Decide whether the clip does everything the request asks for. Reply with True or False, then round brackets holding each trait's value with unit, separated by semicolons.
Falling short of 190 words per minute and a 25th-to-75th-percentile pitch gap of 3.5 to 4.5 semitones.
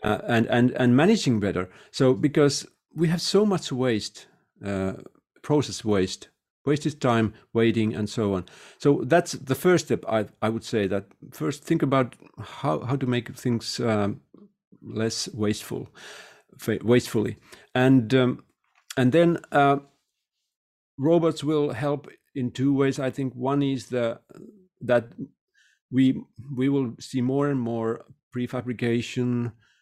True (140 wpm; 3.9 semitones)